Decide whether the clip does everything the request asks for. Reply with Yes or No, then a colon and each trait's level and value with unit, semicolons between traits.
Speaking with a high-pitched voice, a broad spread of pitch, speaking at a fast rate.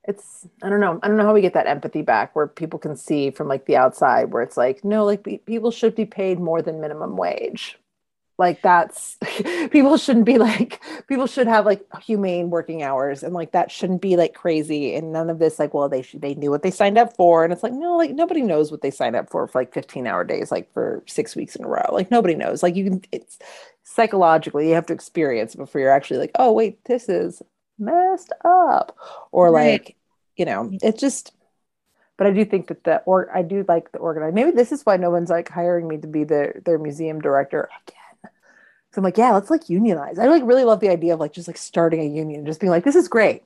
No: medium, 180 Hz; wide, 5.7 semitones; fast, 245 wpm